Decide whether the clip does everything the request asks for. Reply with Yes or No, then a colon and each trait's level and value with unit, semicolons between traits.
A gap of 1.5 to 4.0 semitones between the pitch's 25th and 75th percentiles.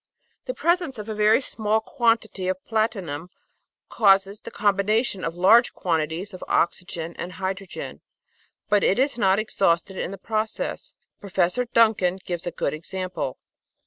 Yes: average, 3.4 semitones